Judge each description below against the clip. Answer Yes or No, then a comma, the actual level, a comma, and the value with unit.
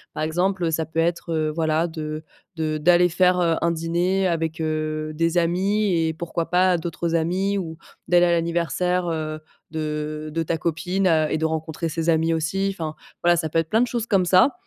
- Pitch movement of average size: No, narrow, 2.0 semitones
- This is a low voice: No, medium, 165 Hz